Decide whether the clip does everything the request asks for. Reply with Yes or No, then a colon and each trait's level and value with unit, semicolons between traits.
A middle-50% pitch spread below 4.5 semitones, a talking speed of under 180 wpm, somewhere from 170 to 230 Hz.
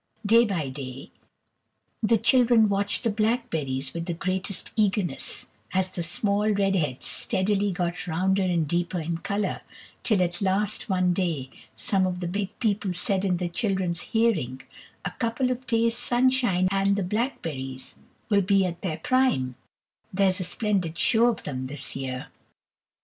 Yes: average, 3.8 semitones; average, 155 wpm; high, 190 Hz